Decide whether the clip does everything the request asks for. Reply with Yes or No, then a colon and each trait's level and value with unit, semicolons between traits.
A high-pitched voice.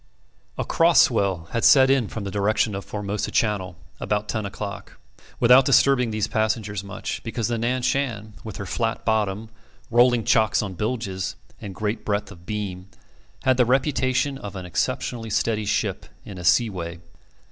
No: low, 110 Hz